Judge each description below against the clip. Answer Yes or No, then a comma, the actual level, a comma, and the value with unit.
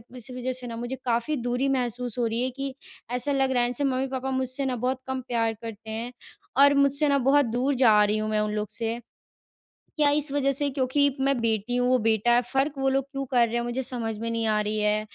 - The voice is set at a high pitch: Yes, high, 245 Hz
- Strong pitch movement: No, average, 2.8 semitones